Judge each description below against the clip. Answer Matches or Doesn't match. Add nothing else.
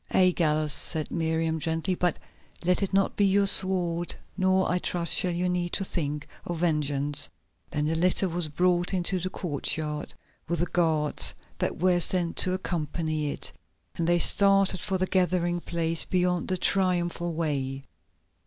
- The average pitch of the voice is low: Doesn't match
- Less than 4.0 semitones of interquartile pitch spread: Matches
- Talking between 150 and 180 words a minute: Matches